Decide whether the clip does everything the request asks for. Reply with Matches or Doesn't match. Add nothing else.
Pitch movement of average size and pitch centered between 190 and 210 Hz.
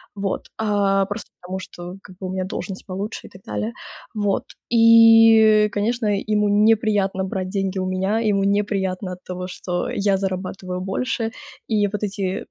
Doesn't match